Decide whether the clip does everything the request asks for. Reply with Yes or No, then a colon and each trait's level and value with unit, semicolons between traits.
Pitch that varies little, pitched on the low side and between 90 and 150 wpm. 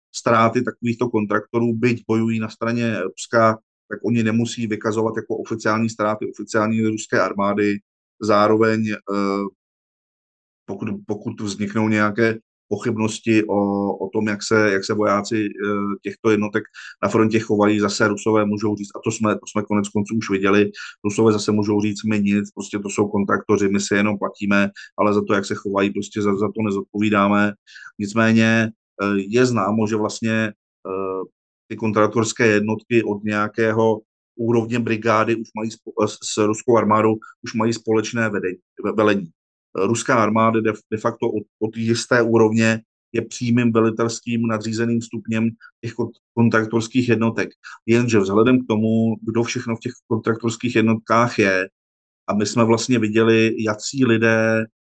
Yes: narrow, 1.6 semitones; low, 110 Hz; average, 145 wpm